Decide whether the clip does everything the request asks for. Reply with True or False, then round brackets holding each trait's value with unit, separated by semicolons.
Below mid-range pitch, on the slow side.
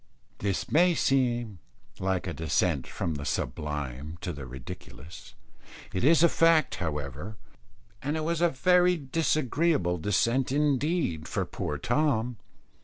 True (115 Hz; 125 wpm)